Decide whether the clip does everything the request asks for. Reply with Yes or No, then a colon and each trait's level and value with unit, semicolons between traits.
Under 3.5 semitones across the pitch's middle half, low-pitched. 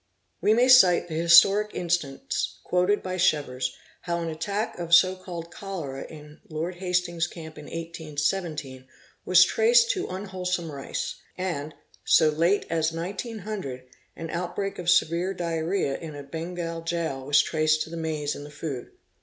No: average, 2.9 semitones; medium, 170 Hz